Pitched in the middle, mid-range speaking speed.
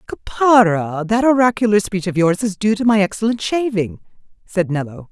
No: high, 205 Hz; average, 165 wpm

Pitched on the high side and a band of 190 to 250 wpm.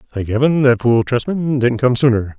No: low, 125 Hz; average, 200 wpm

